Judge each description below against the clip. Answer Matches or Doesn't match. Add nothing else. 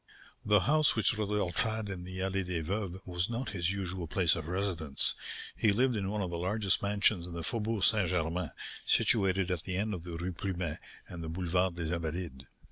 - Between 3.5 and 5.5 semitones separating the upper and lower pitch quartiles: Doesn't match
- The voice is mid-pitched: Doesn't match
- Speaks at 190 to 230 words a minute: Matches